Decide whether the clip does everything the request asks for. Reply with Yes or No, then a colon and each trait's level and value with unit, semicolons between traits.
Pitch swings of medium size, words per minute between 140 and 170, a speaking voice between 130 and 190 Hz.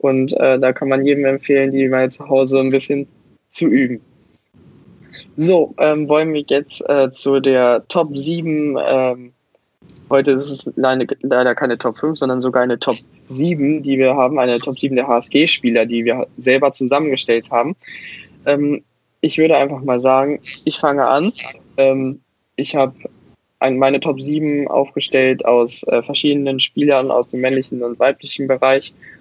No: narrow, 1.8 semitones; average, 160 wpm; low, 135 Hz